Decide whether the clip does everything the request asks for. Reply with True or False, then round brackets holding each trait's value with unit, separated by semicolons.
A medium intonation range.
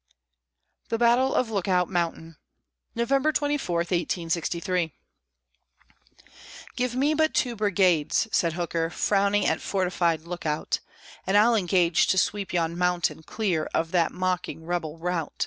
True (3.8 semitones)